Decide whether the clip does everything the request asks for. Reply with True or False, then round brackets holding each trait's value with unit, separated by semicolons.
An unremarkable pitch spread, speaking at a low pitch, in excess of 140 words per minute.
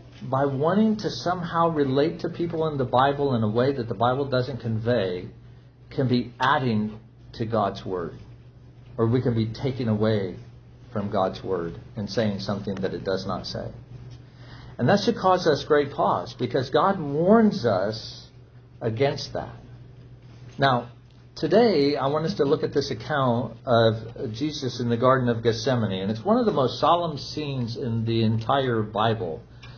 True (3.5 semitones; 125 Hz; 165 wpm)